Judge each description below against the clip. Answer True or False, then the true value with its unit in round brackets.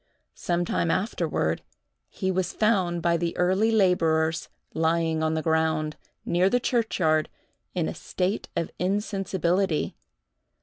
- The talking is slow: True (120 wpm)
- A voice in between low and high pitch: True (175 Hz)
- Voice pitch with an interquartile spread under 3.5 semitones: True (3.0 semitones)